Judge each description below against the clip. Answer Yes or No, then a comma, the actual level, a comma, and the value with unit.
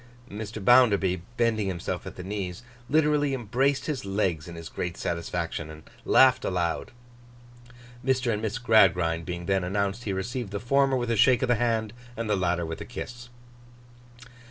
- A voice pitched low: Yes, low, 105 Hz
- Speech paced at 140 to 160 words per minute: No, average, 170 wpm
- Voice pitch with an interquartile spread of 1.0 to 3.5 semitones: No, average, 5.3 semitones